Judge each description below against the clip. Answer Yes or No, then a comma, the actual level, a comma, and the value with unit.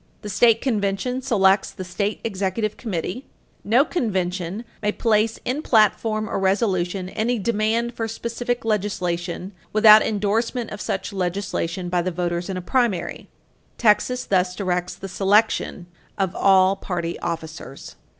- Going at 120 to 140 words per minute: Yes, slow, 135 wpm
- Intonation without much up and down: No, average, 3.6 semitones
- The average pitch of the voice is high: Yes, high, 200 Hz